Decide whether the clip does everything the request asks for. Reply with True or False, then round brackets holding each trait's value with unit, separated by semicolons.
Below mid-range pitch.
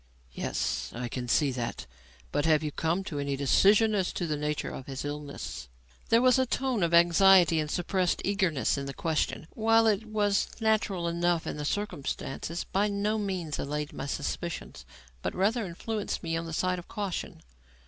False (170 Hz)